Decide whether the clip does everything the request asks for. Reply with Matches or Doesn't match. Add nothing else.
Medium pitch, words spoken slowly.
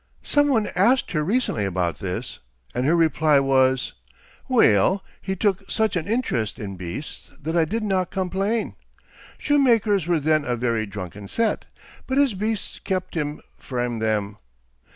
Doesn't match